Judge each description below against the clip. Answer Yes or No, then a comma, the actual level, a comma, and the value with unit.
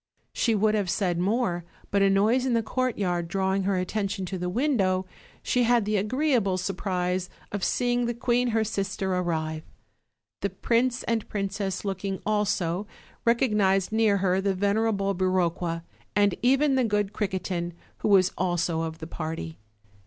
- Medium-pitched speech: No, high, 195 Hz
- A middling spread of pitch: Yes, average, 3.3 semitones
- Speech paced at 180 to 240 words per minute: No, average, 155 wpm